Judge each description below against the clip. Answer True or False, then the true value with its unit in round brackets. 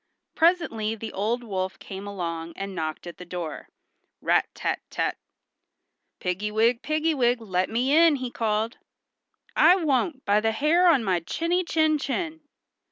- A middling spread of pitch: False (8.0 semitones)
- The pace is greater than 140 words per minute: True (150 wpm)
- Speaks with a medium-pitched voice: False (230 Hz)